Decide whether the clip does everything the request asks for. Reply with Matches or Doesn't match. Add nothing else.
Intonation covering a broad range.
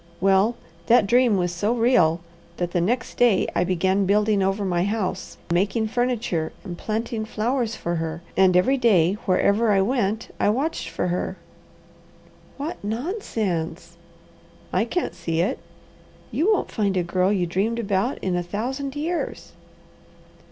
Doesn't match